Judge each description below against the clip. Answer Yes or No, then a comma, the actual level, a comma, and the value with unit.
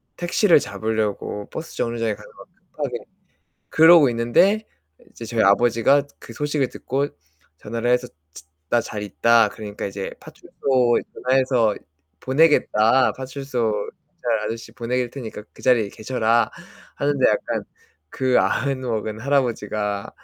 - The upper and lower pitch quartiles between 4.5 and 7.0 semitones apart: No, average, 3.4 semitones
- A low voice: Yes, low, 120 Hz